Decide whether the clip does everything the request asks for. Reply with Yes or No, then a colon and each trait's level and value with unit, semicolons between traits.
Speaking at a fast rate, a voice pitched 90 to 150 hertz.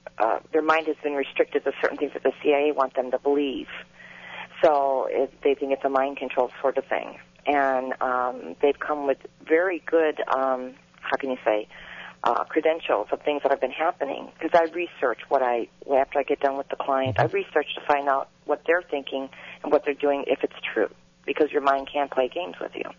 Yes: fast, 215 wpm; medium, 140 Hz